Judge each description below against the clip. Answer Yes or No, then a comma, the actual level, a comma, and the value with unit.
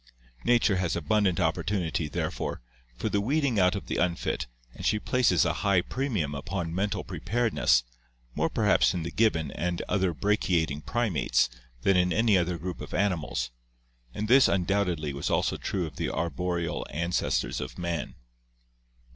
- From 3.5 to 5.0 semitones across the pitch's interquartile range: Yes, average, 3.8 semitones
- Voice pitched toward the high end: No, very low, 90 Hz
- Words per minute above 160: No, average, 155 wpm